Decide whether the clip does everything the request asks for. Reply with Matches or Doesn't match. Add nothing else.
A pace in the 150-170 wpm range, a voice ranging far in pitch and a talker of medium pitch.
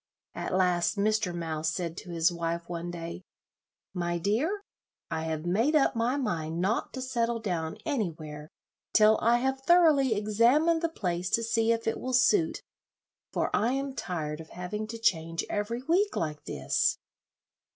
Doesn't match